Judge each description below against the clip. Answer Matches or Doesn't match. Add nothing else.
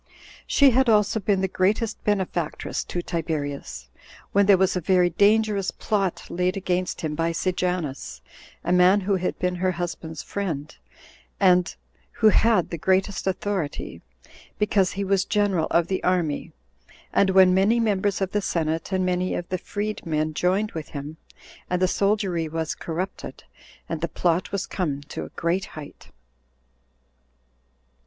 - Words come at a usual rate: Matches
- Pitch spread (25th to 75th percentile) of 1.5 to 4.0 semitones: Matches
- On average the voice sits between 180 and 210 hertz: Matches